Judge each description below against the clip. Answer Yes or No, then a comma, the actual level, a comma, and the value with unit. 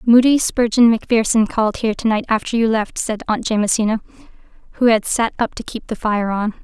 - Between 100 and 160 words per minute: No, average, 190 wpm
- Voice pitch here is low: No, high, 225 Hz